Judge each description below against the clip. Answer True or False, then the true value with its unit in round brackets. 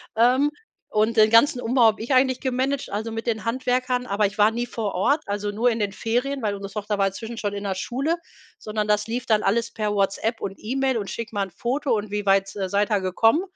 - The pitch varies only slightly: False (3.2 semitones)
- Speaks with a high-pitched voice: True (225 Hz)